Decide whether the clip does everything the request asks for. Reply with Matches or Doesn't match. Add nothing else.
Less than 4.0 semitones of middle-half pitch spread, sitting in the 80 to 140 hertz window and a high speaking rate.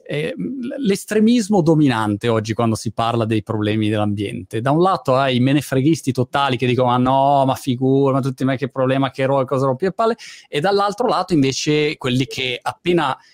Doesn't match